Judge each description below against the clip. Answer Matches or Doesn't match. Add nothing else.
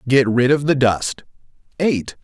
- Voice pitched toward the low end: Matches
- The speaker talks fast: Doesn't match